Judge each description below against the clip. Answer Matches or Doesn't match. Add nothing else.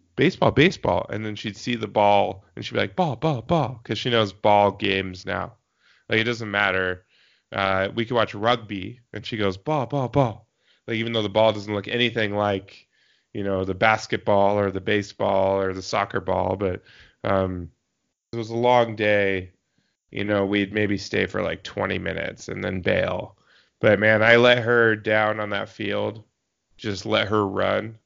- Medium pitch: Doesn't match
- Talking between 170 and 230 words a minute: Matches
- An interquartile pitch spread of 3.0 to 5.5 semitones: Doesn't match